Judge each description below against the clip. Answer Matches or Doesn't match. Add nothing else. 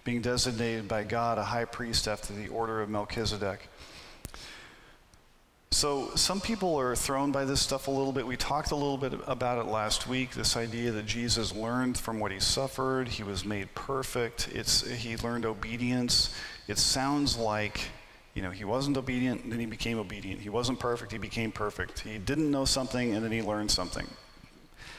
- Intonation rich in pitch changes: Doesn't match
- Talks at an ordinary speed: Matches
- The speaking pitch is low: Matches